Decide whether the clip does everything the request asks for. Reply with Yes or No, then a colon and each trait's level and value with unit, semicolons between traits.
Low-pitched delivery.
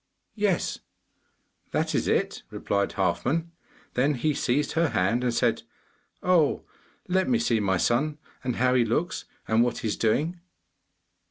Yes: low, 130 Hz